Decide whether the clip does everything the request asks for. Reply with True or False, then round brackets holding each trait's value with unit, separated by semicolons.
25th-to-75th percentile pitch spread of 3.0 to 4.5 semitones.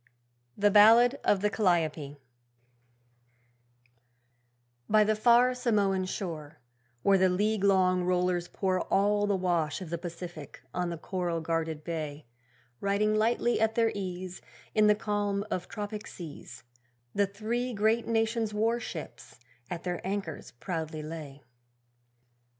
True (3.8 semitones)